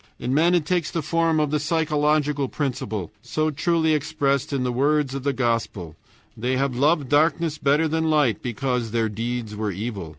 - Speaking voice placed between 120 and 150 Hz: Yes, medium, 140 Hz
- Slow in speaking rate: No, average, 185 wpm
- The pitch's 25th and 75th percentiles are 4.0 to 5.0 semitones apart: Yes, average, 4.3 semitones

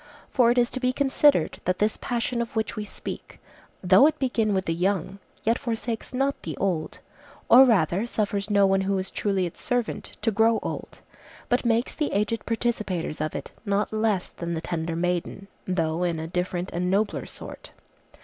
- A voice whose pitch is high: Yes, high, 205 Hz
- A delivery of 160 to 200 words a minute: Yes, average, 190 wpm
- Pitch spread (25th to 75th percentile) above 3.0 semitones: Yes, average, 4.6 semitones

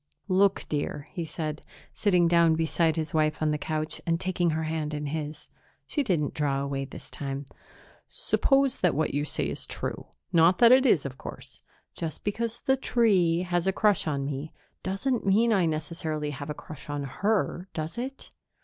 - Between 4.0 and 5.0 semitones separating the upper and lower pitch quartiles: Yes, average, 4.3 semitones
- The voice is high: No, medium, 160 Hz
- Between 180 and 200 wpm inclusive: Yes, average, 185 wpm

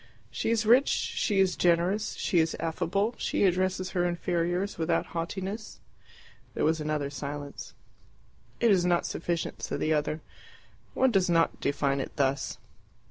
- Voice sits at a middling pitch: Yes, medium, 175 Hz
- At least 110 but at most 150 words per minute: Yes, average, 145 wpm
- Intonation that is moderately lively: Yes, average, 3.4 semitones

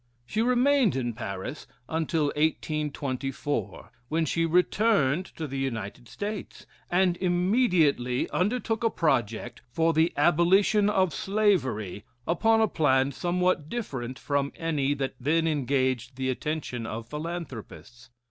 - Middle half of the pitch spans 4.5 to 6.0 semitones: Yes, wide, 5.6 semitones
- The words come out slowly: Yes, slow, 120 wpm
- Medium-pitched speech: Yes, medium, 155 Hz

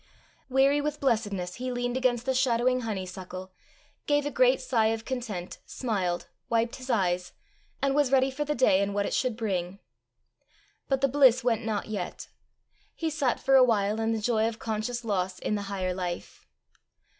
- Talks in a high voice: Yes, high, 230 Hz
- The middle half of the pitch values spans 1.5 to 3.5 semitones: No, average, 4.5 semitones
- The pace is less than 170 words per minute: No, average, 180 wpm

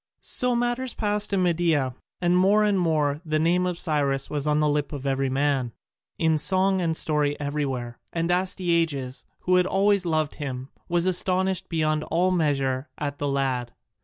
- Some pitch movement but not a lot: Yes, average, 4.2 semitones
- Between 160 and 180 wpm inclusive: Yes, average, 170 wpm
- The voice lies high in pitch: No, medium, 160 Hz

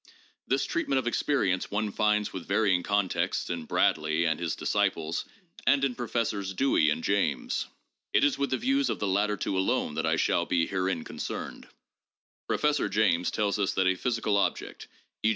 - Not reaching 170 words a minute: No, average, 175 wpm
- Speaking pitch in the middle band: No, low, 100 Hz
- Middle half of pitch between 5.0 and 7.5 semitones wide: No, average, 4.6 semitones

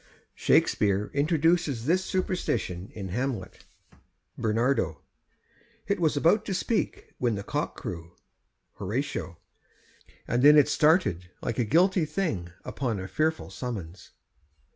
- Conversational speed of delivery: No, slow, 120 wpm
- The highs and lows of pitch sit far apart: Yes, wide, 8.4 semitones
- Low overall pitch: Yes, low, 125 Hz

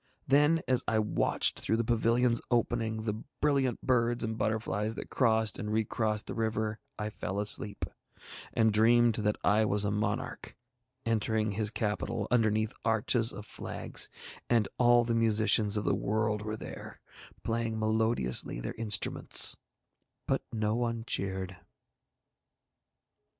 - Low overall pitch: Yes, low, 110 Hz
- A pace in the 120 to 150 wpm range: Yes, average, 140 wpm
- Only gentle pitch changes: Yes, narrow, 1.6 semitones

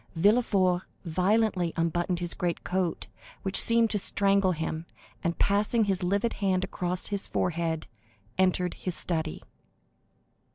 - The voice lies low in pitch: No, medium, 185 Hz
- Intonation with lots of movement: No, average, 2.7 semitones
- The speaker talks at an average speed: No, slow, 120 wpm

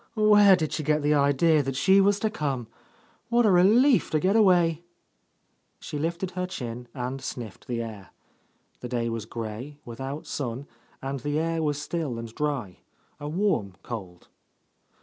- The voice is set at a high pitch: No, medium, 145 Hz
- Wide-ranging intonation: Yes, wide, 6.5 semitones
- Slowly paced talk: No, average, 165 wpm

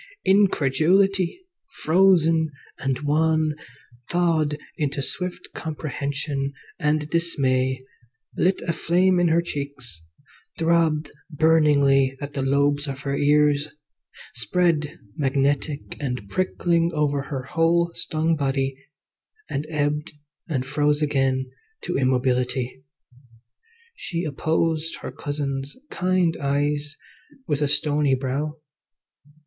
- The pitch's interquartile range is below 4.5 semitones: Yes, average, 2.9 semitones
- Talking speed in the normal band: No, slow, 100 wpm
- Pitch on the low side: No, medium, 150 Hz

